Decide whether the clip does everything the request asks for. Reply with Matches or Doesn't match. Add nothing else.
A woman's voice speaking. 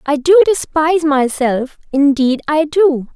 Matches